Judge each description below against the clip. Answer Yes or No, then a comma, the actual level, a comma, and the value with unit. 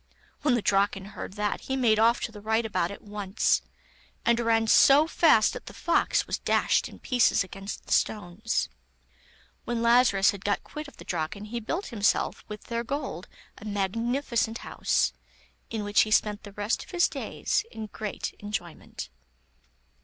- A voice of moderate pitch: No, high, 220 Hz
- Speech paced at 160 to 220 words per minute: Yes, average, 170 wpm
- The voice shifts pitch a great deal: No, average, 2.7 semitones